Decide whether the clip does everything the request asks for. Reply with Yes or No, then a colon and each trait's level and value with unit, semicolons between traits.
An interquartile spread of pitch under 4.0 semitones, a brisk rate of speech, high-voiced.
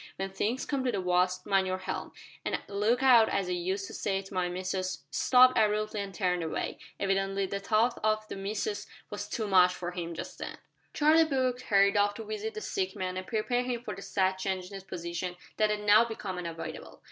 Yes: average, 3.5 semitones; fast, 225 wpm; high, 200 Hz